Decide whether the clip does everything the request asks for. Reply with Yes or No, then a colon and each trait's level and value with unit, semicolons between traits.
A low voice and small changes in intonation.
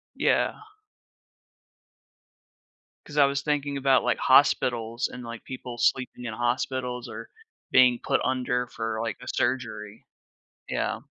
Yes: low, 125 Hz; narrow, 2.0 semitones